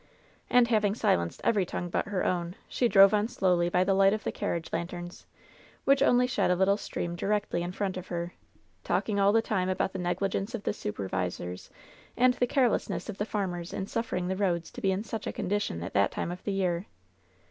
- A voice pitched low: No, high, 190 Hz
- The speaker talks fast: Yes, fast, 215 wpm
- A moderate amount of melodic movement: Yes, average, 3.3 semitones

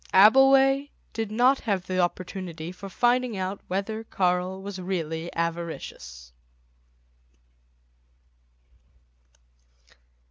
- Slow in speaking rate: Yes, slow, 80 wpm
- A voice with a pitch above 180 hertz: Yes, high, 190 Hz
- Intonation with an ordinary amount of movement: Yes, average, 4.2 semitones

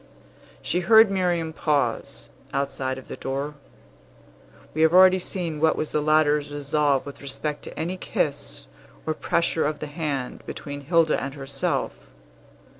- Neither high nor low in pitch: Yes, medium, 150 Hz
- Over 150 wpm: No, average, 145 wpm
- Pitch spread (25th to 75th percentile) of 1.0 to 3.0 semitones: Yes, average, 2.7 semitones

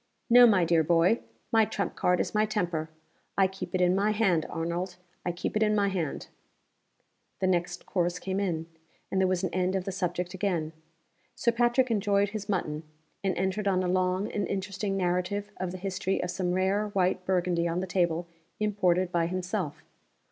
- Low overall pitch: No, medium, 185 Hz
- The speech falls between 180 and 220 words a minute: Yes, average, 190 wpm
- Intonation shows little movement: Yes, narrow, 2.2 semitones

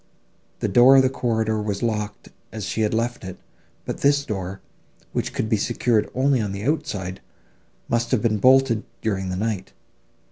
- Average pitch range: Yes, average, 3.5 semitones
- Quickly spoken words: No, average, 175 wpm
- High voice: No, low, 110 Hz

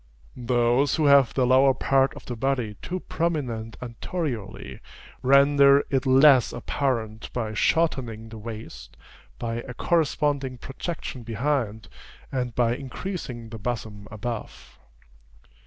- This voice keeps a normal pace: No, slow, 120 wpm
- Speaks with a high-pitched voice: No, low, 125 Hz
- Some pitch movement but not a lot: Yes, average, 3.4 semitones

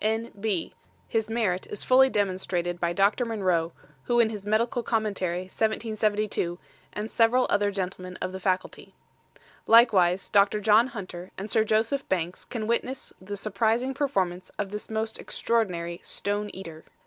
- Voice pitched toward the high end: Yes, high, 210 Hz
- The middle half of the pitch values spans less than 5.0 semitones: Yes, average, 3.3 semitones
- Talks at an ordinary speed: Yes, average, 150 wpm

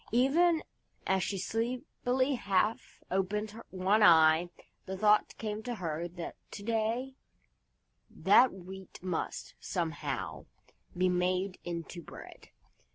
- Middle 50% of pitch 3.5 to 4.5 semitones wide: Yes, average, 4.1 semitones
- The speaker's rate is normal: No, slow, 110 wpm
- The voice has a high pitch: Yes, high, 195 Hz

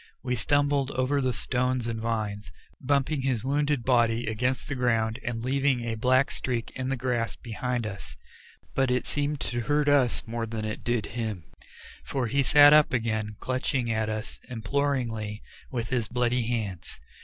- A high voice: No, low, 125 Hz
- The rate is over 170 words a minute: No, average, 165 wpm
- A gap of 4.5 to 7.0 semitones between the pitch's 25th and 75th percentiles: No, average, 2.9 semitones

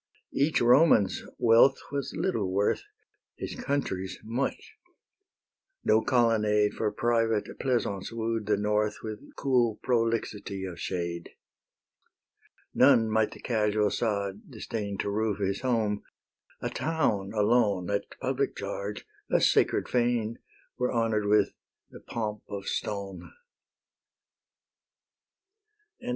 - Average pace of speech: No, slow, 110 wpm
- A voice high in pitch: No, low, 110 Hz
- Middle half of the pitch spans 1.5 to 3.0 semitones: Yes, average, 2.7 semitones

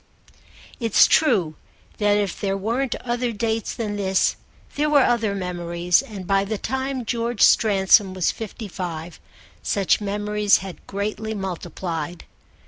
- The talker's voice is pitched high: Yes, high, 205 Hz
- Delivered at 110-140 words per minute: Yes, slow, 135 wpm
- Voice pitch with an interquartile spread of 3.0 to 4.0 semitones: Yes, average, 3.3 semitones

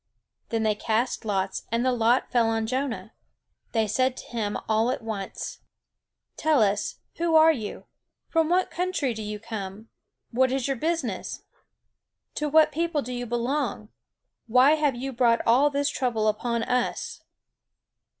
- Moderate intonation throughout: Yes, average, 4.2 semitones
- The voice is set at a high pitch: Yes, high, 245 Hz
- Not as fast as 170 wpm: Yes, average, 155 wpm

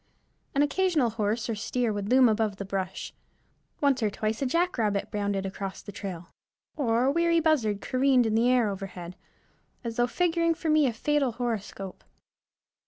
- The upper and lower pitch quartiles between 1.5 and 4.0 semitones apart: No, average, 5.3 semitones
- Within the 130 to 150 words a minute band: No, average, 170 wpm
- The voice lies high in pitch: Yes, high, 230 Hz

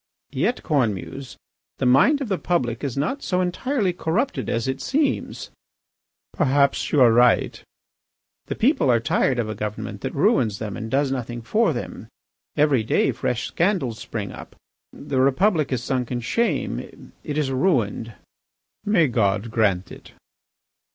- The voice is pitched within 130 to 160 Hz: Yes, low, 135 Hz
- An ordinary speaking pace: Yes, average, 150 wpm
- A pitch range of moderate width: No, wide, 7.1 semitones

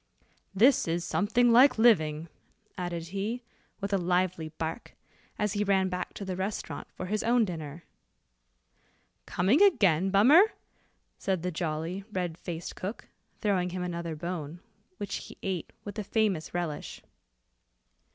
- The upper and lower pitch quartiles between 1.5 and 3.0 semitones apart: No, average, 3.5 semitones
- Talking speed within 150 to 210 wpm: No, average, 140 wpm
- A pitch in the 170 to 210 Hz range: Yes, medium, 185 Hz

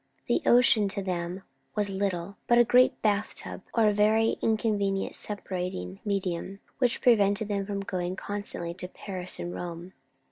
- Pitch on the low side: No, high, 200 Hz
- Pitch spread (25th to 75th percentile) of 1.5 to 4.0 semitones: Yes, narrow, 2.6 semitones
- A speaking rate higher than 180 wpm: No, average, 155 wpm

